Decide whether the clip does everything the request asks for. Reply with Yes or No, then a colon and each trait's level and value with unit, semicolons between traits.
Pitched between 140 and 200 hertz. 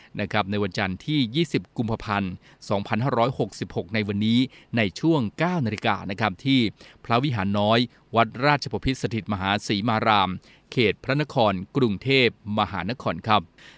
No: low, 115 Hz